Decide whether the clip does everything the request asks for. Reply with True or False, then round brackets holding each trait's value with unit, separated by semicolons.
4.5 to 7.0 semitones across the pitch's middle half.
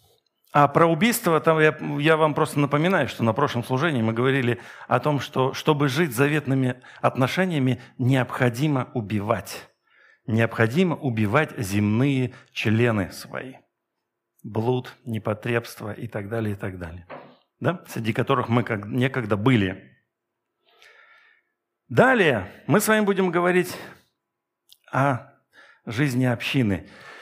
True (5.0 semitones)